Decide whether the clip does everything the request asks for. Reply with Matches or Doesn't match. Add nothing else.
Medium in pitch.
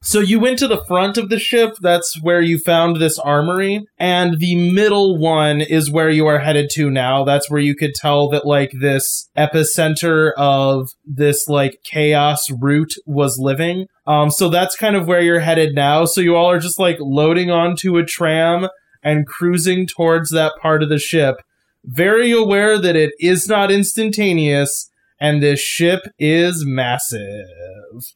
Matches